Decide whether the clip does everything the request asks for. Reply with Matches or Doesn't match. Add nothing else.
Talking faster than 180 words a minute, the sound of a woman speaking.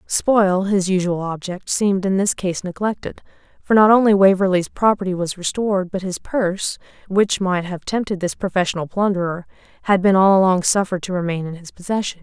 Doesn't match